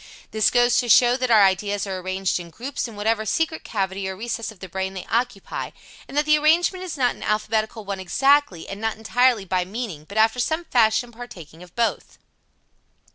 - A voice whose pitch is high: Yes, high, 220 Hz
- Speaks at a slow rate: No, average, 200 wpm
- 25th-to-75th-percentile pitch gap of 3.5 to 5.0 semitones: Yes, average, 4.3 semitones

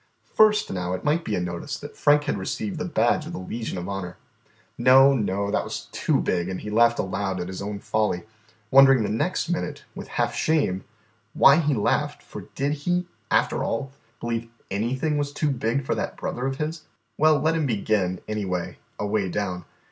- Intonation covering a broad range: Yes, wide, 6.9 semitones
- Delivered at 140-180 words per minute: No, average, 195 wpm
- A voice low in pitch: Yes, low, 115 Hz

